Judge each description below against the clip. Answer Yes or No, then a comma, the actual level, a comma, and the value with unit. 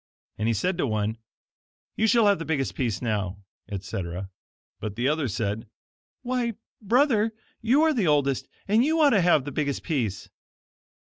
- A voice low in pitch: No, medium, 145 Hz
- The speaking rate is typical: Yes, average, 165 wpm